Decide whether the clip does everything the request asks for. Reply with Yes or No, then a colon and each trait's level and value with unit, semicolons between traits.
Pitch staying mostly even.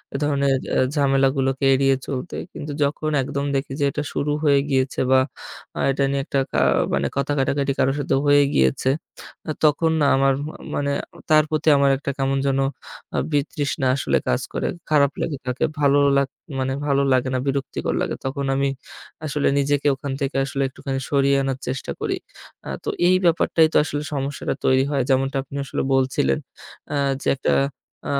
Yes: narrow, 1.2 semitones